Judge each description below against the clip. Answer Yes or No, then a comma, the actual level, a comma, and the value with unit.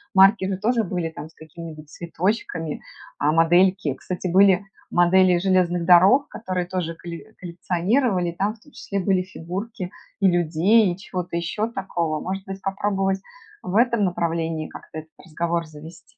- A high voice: No, medium, 180 Hz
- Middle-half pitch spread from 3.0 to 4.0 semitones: No, narrow, 2.5 semitones